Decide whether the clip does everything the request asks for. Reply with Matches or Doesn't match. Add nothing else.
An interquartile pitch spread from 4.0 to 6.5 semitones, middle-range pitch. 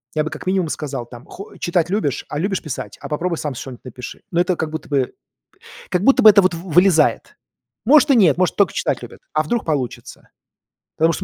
Matches